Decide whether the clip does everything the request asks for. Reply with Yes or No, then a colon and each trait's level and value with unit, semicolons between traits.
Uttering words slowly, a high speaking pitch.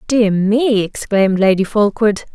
Yes: slow, 130 wpm; high, 210 Hz